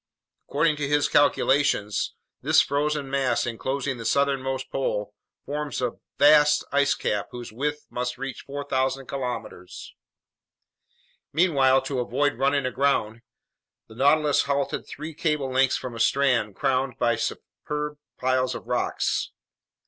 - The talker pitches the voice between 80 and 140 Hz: Yes, low, 135 Hz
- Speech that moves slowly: Yes, slow, 125 wpm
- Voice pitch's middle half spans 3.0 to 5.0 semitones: No, narrow, 2.4 semitones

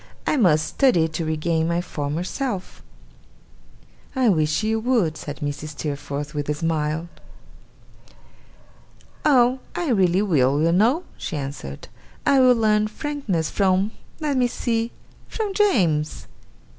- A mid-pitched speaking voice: Yes, medium, 180 Hz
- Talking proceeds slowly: Yes, slow, 130 wpm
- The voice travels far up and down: Yes, wide, 7.9 semitones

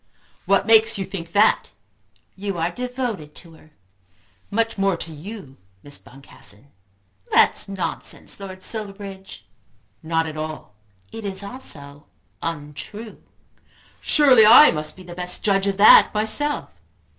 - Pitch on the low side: No, high, 195 Hz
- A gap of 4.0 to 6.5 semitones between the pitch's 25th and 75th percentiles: Yes, average, 5.2 semitones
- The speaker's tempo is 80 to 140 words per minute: Yes, slow, 135 wpm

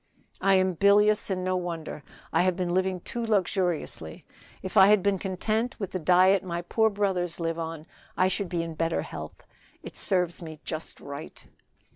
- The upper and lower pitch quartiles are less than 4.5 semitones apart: Yes, average, 2.7 semitones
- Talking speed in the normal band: Yes, average, 180 wpm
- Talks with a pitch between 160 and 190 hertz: Yes, medium, 185 Hz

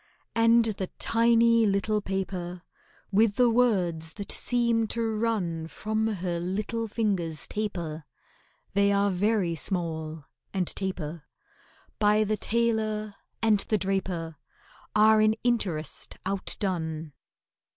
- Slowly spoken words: Yes, slow, 110 wpm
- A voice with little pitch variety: No, average, 4.0 semitones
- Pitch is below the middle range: No, high, 200 Hz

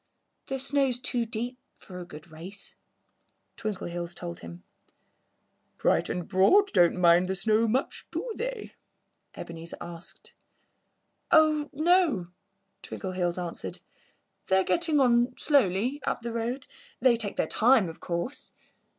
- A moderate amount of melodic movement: No, wide, 7.3 semitones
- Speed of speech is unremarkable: No, slow, 125 wpm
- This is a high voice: Yes, high, 220 Hz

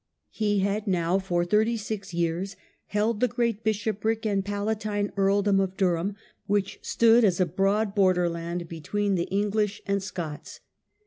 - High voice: Yes, high, 200 Hz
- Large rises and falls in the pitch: No, narrow, 2.4 semitones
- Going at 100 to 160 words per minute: Yes, average, 145 wpm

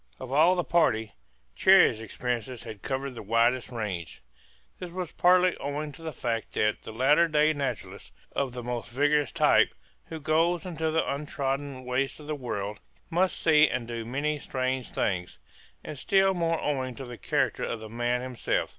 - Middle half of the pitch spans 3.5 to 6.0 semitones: Yes, average, 4.5 semitones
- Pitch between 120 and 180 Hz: Yes, low, 135 Hz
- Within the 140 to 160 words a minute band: No, average, 175 wpm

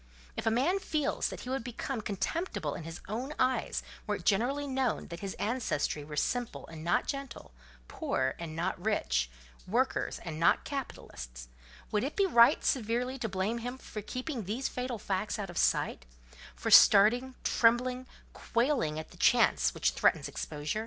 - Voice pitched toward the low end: No, high, 220 Hz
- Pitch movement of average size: No, wide, 7.4 semitones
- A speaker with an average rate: Yes, average, 165 wpm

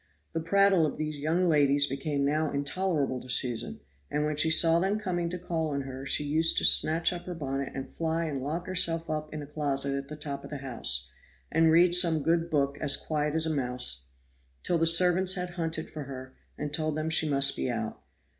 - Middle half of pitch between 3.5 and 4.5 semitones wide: No, average, 3.0 semitones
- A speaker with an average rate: No, fast, 220 wpm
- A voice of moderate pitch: Yes, medium, 155 Hz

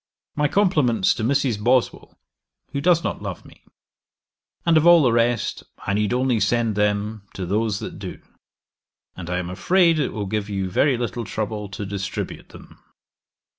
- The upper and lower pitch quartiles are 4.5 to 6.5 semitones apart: Yes, average, 5.2 semitones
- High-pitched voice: No, low, 115 Hz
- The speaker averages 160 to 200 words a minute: Yes, average, 170 wpm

